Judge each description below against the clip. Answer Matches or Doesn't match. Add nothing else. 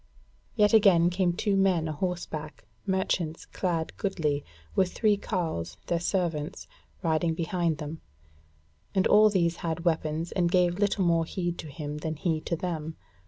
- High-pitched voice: Doesn't match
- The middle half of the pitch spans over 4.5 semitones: Doesn't match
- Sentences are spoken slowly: Doesn't match